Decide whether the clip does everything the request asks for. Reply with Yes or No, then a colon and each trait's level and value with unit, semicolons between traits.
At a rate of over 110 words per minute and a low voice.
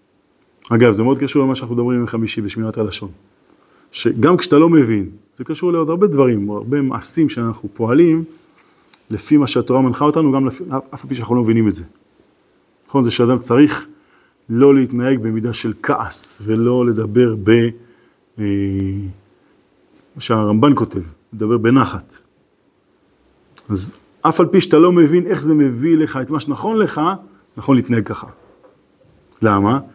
Yes: fast, 150 wpm; low, 125 Hz